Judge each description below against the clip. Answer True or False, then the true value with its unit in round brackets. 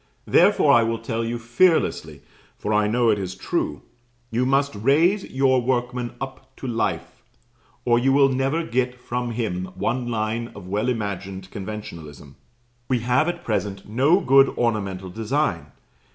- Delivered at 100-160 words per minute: True (150 wpm)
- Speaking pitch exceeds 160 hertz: False (120 Hz)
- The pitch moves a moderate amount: True (4.1 semitones)